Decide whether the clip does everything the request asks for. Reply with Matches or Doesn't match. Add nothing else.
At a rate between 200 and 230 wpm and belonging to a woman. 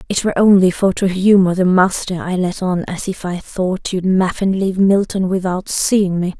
Matches